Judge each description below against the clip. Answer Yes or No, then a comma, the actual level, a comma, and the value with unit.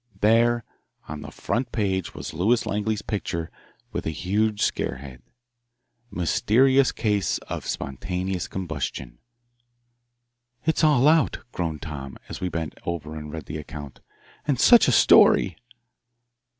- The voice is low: Yes, very low, 95 Hz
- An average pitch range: No, wide, 6.6 semitones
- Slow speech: Yes, slow, 130 wpm